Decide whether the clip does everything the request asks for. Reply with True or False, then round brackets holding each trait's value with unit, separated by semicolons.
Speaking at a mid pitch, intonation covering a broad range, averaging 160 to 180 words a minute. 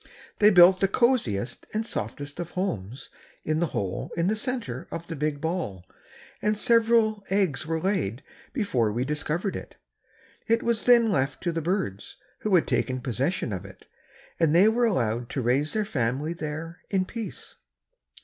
True (165 Hz; 8.0 semitones; 170 wpm)